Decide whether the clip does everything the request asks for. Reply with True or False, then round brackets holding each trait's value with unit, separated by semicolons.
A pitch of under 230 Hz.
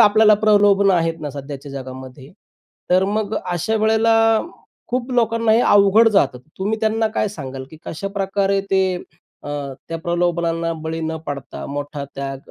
True (190 Hz)